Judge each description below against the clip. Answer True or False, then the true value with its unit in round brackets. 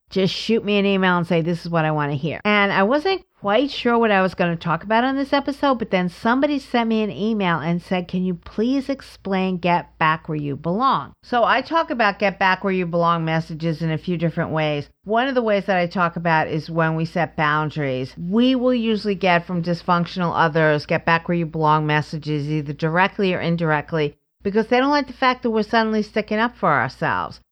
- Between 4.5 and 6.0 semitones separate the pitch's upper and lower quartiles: True (5.4 semitones)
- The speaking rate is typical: False (230 wpm)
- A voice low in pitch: False (180 Hz)